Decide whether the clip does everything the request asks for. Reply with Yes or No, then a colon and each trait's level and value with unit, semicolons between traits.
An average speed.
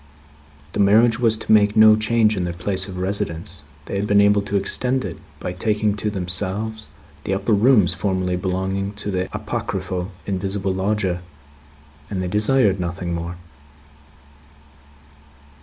Yes: average, 145 wpm